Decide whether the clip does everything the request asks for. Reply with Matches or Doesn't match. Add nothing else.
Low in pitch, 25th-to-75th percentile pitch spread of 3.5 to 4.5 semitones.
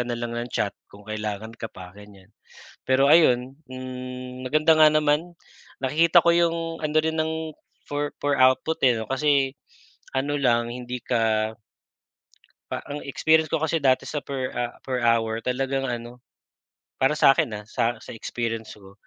Matches